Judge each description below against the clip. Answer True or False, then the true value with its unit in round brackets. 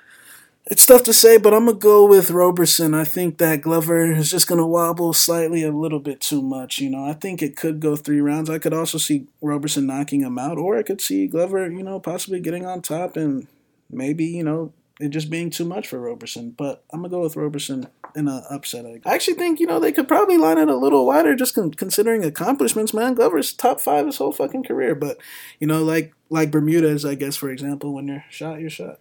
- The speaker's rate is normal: False (230 wpm)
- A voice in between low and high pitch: True (160 Hz)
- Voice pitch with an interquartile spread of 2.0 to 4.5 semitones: True (3.7 semitones)